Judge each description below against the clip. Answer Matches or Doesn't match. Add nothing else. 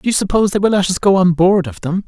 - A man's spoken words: Matches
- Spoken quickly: Matches